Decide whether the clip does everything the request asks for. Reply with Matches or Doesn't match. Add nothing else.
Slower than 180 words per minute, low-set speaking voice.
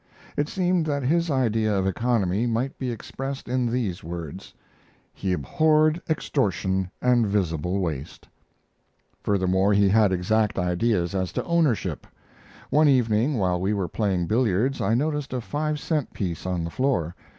Matches